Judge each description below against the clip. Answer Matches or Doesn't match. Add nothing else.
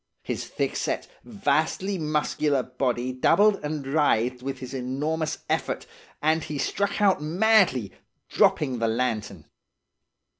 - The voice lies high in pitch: Doesn't match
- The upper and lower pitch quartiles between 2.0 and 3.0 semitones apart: Doesn't match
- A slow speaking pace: Matches